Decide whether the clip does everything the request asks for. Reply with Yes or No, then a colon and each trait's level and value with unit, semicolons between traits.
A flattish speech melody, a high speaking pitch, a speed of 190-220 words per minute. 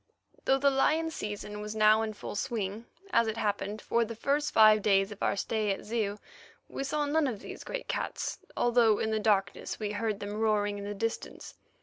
Yes: narrow, 2.2 semitones; high, 215 Hz; fast, 205 wpm